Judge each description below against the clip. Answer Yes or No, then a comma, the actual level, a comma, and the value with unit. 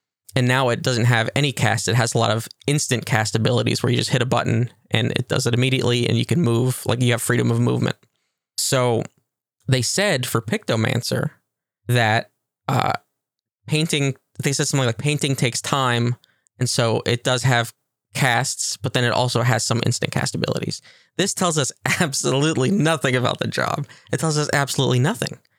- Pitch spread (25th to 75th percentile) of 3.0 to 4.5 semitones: Yes, average, 3.4 semitones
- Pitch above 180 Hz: No, low, 125 Hz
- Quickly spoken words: No, average, 185 wpm